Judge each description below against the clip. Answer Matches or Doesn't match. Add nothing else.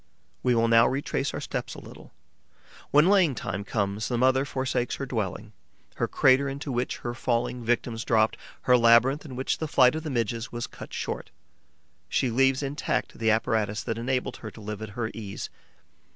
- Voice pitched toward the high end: Doesn't match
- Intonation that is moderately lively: Matches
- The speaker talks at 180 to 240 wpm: Matches